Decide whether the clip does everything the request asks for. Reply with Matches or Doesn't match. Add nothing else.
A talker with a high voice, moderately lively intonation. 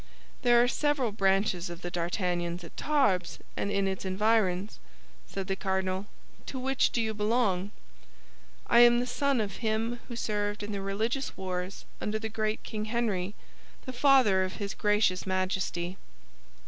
Matches